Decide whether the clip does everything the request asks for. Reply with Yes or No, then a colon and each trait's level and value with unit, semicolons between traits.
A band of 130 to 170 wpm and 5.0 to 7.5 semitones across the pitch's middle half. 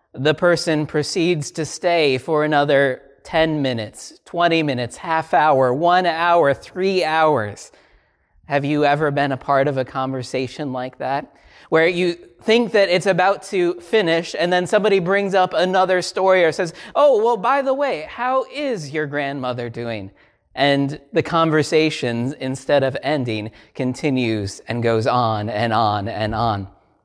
Yes: average, 155 wpm; wide, 5.6 semitones